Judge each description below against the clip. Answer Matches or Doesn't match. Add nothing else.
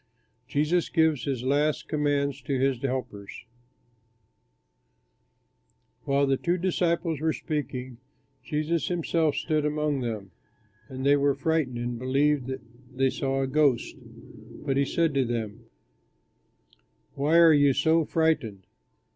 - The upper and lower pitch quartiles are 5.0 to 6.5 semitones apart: Doesn't match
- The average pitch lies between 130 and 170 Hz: Matches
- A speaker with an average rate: Doesn't match